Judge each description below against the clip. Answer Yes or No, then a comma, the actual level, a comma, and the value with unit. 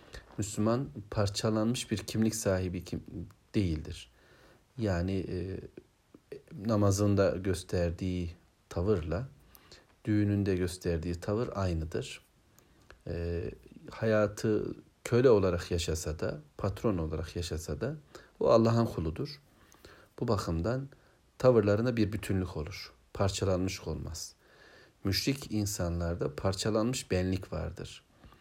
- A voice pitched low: Yes, low, 100 Hz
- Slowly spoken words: Yes, slow, 90 wpm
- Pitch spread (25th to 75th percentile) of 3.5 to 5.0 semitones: Yes, average, 3.8 semitones